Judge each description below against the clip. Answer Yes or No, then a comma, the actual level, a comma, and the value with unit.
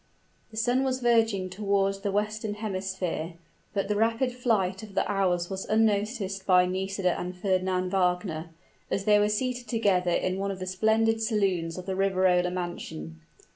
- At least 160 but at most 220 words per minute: Yes, average, 165 wpm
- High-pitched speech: Yes, high, 195 Hz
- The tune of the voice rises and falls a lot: No, average, 2.9 semitones